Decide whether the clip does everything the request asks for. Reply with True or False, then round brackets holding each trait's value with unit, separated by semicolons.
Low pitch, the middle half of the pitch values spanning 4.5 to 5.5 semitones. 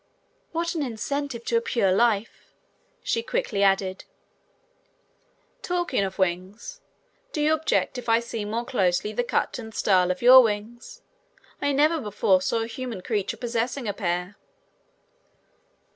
False (230 Hz; 4.9 semitones)